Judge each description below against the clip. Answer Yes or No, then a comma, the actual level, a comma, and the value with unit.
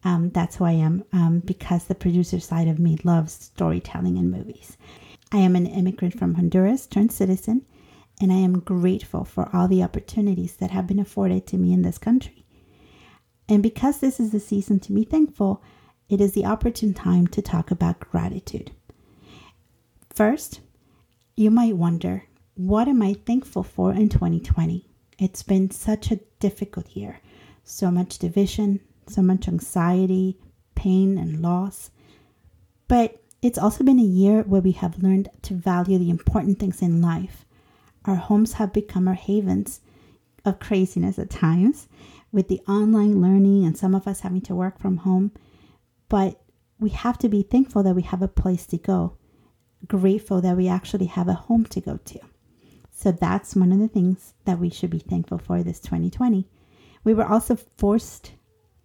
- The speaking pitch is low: No, high, 190 Hz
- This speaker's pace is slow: No, average, 170 wpm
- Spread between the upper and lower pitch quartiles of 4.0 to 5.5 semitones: No, average, 2.8 semitones